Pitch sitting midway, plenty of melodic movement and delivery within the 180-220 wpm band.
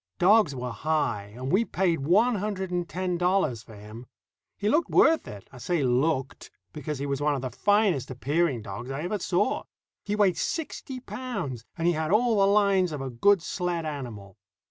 Yes: medium, 165 Hz; wide, 7.2 semitones; average, 190 wpm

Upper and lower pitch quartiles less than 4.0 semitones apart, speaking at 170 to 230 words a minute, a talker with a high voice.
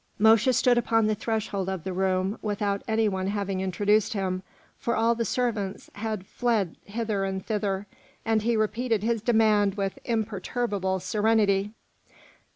No: narrow, 2.5 semitones; average, 150 wpm; high, 210 Hz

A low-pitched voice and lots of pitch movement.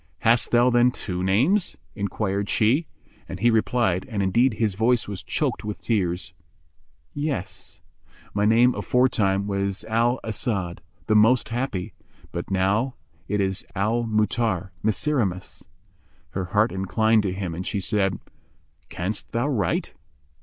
No: low, 105 Hz; average, 3.8 semitones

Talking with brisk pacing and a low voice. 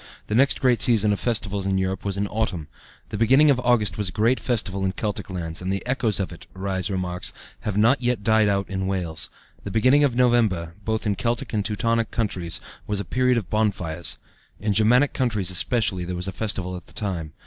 Yes: fast, 215 wpm; low, 105 Hz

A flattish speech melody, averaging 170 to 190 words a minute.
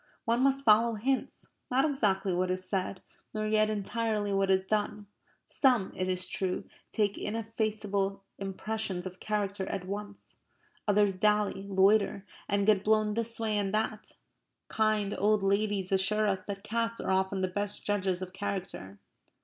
No: narrow, 2.0 semitones; average, 155 wpm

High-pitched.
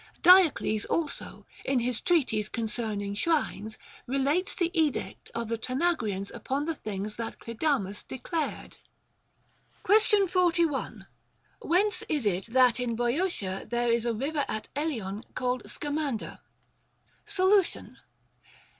Yes: very high, 260 Hz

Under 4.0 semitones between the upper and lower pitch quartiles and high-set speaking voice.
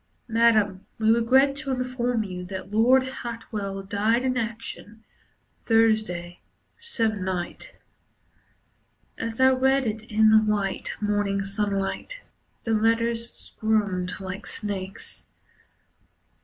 Yes: average, 3.0 semitones; high, 220 Hz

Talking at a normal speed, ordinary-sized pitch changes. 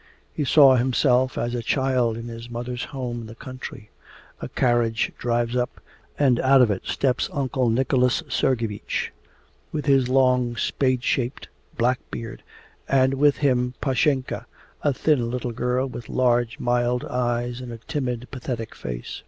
No: average, 155 wpm; narrow, 1.7 semitones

